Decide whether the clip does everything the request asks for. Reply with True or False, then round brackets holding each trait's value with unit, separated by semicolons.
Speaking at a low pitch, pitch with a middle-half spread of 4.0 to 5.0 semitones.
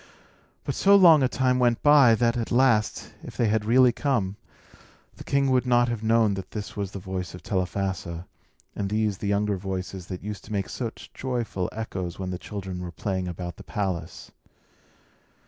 True (105 Hz; 4.4 semitones)